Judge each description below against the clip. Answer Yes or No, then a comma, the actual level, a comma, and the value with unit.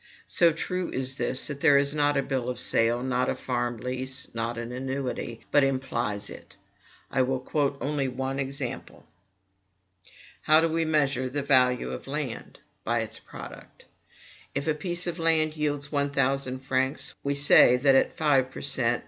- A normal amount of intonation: No, narrow, 2.3 semitones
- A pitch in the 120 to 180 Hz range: Yes, low, 135 Hz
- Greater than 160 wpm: Yes, average, 175 wpm